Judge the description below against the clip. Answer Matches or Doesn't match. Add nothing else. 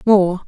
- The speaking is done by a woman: Matches